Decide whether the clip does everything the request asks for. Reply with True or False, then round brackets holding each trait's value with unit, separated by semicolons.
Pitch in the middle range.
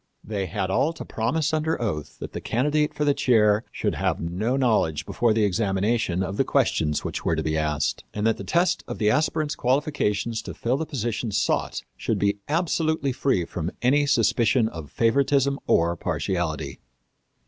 False (115 Hz)